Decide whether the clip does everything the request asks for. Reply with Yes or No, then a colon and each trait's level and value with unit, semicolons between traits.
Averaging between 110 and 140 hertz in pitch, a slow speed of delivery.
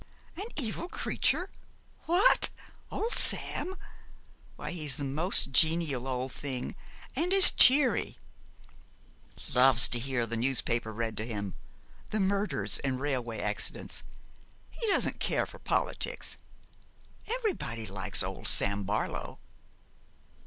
Yes: low, 135 Hz; slow, 115 wpm